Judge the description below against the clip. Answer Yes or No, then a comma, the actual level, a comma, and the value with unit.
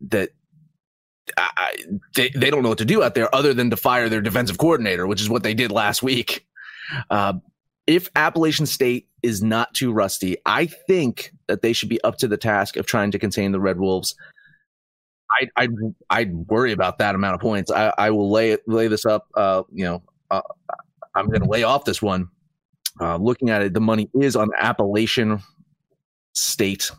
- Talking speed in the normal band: Yes, average, 195 wpm